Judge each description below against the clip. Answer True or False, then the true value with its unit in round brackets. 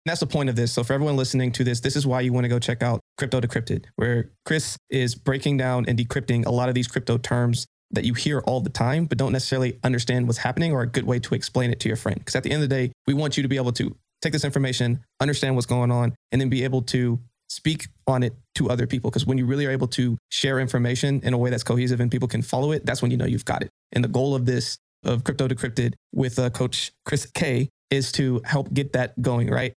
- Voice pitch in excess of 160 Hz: False (125 Hz)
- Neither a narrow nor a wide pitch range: False (1.9 semitones)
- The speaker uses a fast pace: True (275 wpm)